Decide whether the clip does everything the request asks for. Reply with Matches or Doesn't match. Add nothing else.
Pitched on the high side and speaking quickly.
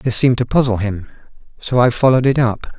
Doesn't match